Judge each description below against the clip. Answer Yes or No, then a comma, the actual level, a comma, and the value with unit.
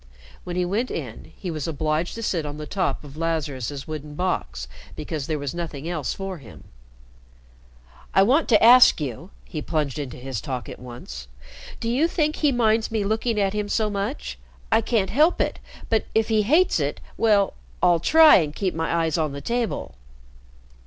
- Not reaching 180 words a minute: No, average, 185 wpm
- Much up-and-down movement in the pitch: Yes, wide, 6.9 semitones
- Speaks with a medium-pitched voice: Yes, medium, 170 Hz